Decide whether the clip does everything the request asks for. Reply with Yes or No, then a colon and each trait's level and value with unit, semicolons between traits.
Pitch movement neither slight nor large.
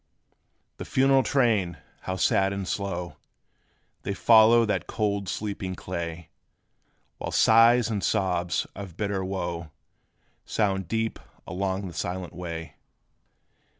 Yes: average, 3.5 semitones